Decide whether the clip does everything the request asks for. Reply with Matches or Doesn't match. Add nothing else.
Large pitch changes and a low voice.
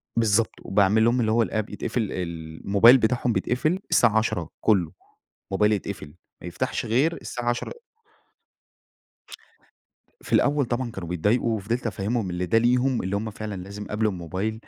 Doesn't match